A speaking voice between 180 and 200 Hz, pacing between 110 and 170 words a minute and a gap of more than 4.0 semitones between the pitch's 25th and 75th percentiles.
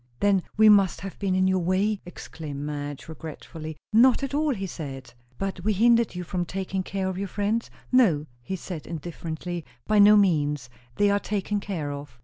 No: medium, 185 Hz; average, 185 wpm; average, 4.4 semitones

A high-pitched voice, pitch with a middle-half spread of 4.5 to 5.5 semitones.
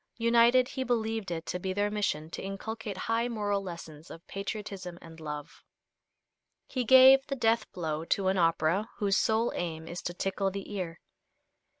Yes: high, 195 Hz; average, 4.8 semitones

